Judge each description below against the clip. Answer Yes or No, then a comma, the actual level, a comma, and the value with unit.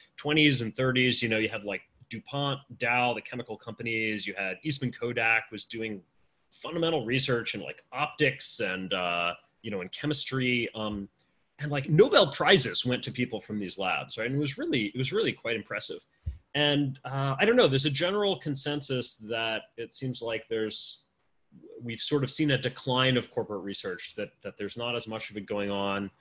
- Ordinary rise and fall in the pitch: Yes, average, 4.0 semitones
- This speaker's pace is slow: No, average, 190 wpm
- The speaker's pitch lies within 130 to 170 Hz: No, low, 120 Hz